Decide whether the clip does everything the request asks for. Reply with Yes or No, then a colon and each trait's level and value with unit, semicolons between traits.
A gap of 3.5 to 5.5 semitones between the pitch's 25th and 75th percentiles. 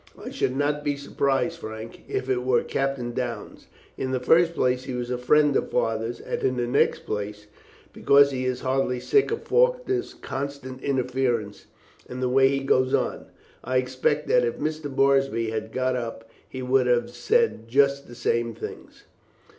No: narrow, 2.4 semitones